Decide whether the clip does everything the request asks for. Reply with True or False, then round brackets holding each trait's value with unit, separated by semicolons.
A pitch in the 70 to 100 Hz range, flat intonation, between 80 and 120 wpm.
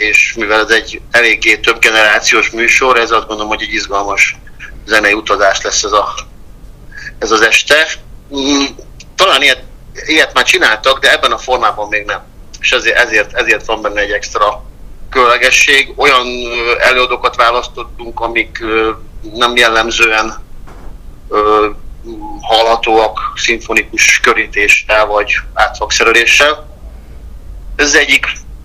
False (110 Hz; 2.2 semitones; 115 wpm)